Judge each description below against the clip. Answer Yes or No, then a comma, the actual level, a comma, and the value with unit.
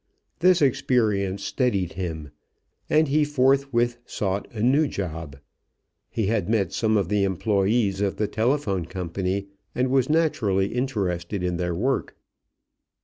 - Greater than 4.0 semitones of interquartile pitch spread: Yes, average, 5.1 semitones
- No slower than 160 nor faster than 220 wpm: No, slow, 135 wpm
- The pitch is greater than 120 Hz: No, low, 105 Hz